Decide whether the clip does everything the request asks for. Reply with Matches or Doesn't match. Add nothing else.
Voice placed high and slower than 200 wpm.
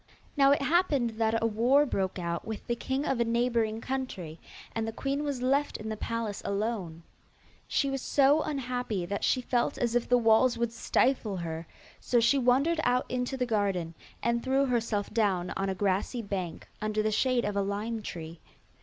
Matches